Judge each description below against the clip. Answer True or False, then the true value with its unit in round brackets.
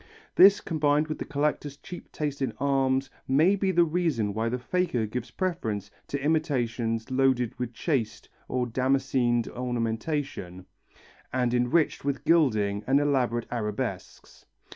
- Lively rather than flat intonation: False (4.3 semitones)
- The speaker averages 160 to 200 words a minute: False (135 wpm)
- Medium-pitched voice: False (130 Hz)